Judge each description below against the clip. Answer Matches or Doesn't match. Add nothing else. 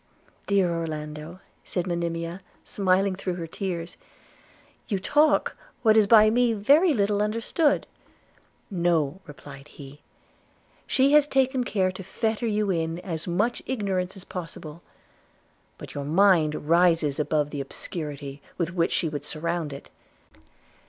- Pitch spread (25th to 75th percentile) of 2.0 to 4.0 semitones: Doesn't match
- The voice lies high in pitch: Doesn't match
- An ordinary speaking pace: Doesn't match